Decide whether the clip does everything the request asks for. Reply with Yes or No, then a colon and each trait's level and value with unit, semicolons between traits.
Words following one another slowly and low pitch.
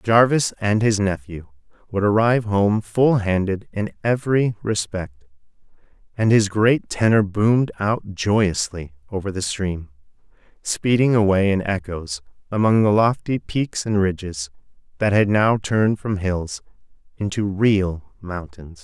Yes: slow, 130 wpm; low, 100 Hz